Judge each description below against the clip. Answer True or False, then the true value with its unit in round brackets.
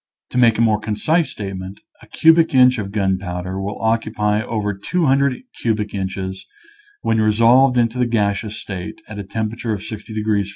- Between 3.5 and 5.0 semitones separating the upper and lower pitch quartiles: False (2.7 semitones)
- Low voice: True (110 Hz)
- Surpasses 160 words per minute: True (175 wpm)